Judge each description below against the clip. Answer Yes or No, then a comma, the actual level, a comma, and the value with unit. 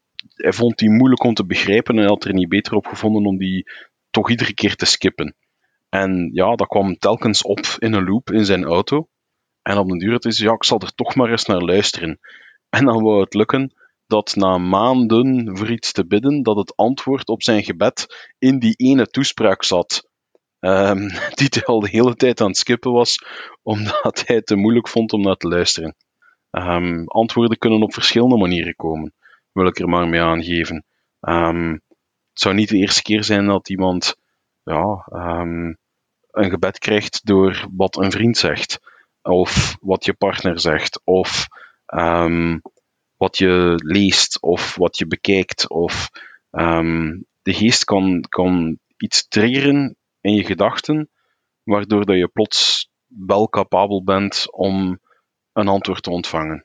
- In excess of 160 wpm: Yes, average, 170 wpm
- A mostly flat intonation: No, average, 3.9 semitones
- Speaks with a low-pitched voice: Yes, low, 100 Hz